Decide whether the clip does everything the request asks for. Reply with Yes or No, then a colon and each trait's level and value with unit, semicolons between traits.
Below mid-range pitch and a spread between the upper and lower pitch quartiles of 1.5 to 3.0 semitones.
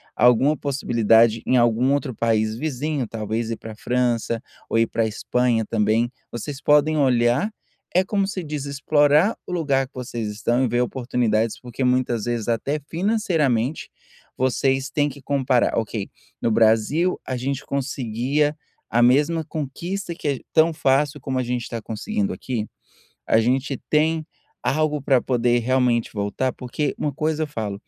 No: low, 130 Hz; average, 4.1 semitones